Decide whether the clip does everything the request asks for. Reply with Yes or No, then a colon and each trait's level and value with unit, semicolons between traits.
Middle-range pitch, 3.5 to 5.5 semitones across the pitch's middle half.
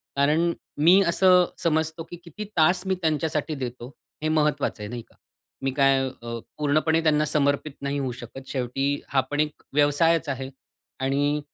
No: medium, 150 Hz; average, 2.8 semitones